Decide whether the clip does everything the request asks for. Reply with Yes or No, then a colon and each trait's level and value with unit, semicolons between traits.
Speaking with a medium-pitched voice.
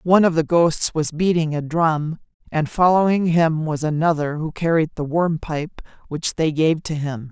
Yes: medium, 160 Hz